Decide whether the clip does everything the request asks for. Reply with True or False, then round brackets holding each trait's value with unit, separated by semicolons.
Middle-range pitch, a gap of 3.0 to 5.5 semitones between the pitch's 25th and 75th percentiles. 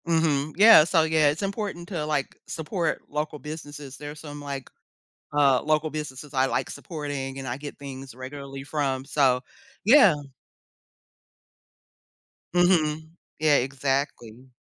False (145 Hz; 2.6 semitones)